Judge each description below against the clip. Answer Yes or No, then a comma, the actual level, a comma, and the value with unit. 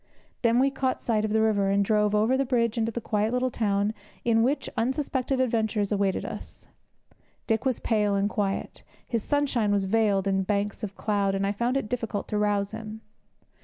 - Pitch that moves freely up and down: No, average, 2.7 semitones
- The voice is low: No, high, 215 Hz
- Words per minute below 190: No, average, 200 wpm